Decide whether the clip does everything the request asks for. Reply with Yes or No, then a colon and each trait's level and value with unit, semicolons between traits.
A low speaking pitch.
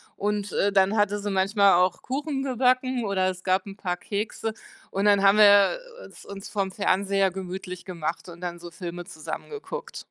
No: high, 195 Hz